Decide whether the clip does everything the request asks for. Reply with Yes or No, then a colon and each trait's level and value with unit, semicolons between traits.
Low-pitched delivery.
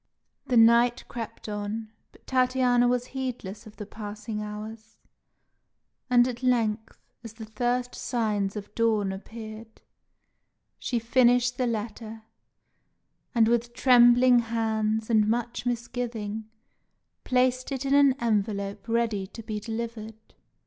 No: high, 230 Hz